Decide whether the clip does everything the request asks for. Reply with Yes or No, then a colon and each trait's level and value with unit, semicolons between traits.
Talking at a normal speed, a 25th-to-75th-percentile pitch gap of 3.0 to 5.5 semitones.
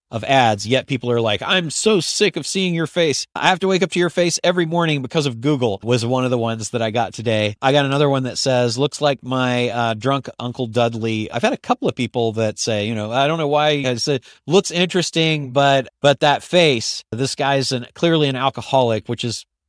No: fast, 240 wpm; average, 4.2 semitones